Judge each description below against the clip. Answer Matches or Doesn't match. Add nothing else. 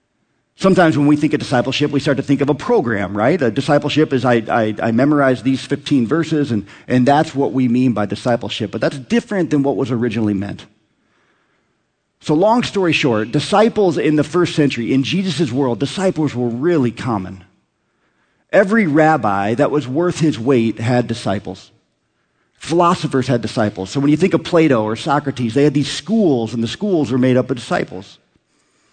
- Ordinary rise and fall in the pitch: Matches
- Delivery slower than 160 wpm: Doesn't match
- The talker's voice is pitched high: Doesn't match